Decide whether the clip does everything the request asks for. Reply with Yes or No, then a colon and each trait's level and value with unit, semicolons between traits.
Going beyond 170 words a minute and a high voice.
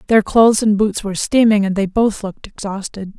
Yes: fast, 205 wpm; high, 205 Hz